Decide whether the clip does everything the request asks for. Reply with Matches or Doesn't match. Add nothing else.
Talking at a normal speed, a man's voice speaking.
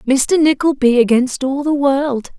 Doesn't match